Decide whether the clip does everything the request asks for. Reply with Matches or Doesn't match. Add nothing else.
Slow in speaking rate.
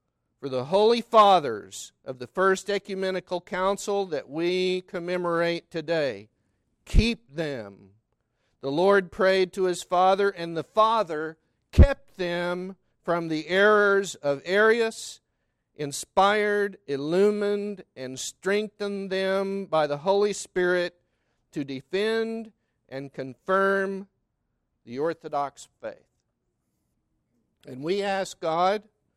Matches